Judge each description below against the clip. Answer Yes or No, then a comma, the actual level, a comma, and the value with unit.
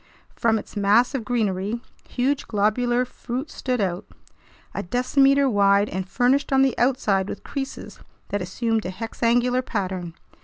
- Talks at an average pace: Yes, average, 145 wpm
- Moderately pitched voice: No, high, 235 Hz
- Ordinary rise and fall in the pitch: Yes, average, 4.0 semitones